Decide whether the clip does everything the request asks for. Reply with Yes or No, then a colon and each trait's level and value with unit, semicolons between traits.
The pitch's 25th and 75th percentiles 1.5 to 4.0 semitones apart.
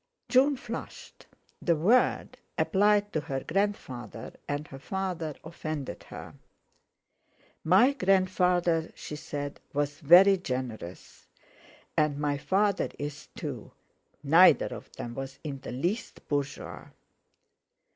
No: average, 5.2 semitones